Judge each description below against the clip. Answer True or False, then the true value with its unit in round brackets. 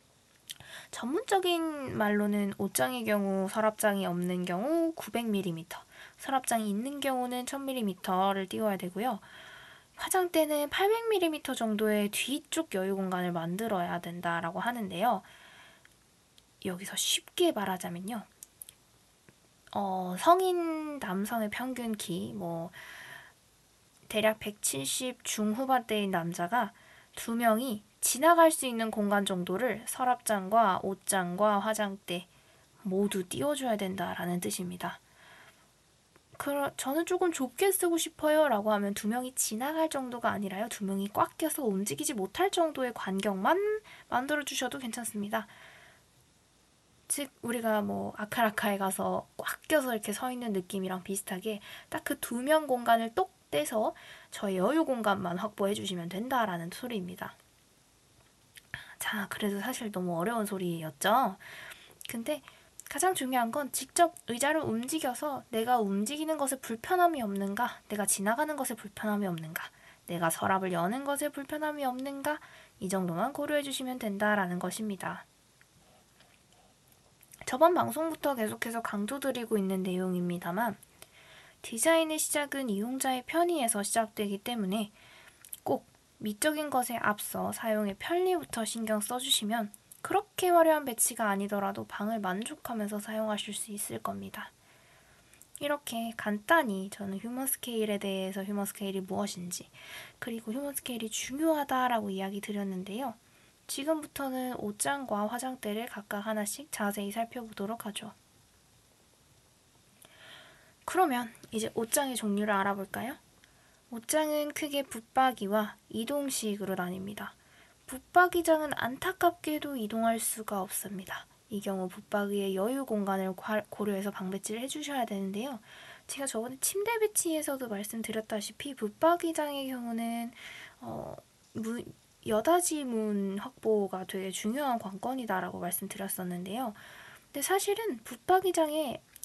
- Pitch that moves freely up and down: True (5.8 semitones)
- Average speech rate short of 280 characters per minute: False (290 characters per minute)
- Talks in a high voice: True (225 Hz)